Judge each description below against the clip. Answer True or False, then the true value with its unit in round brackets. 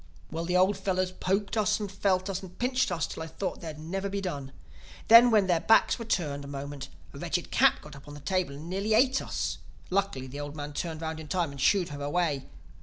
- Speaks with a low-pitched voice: False (180 Hz)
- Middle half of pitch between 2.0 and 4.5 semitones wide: False (5.2 semitones)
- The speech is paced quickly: True (240 wpm)